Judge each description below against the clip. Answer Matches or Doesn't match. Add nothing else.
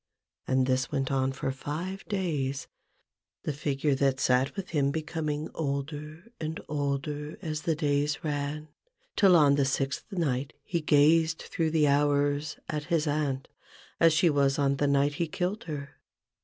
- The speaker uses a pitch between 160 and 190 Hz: Doesn't match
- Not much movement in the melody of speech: Matches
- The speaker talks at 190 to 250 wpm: Doesn't match